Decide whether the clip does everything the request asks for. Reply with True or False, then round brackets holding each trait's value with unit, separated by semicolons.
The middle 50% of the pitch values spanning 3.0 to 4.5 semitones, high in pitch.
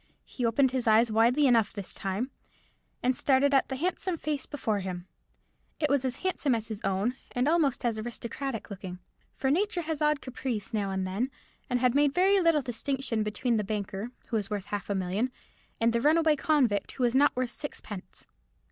False (4.9 semitones; 245 Hz)